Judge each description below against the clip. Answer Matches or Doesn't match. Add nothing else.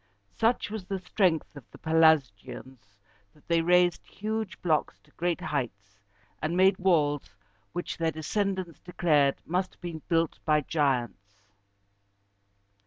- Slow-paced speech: Matches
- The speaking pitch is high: Doesn't match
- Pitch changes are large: Doesn't match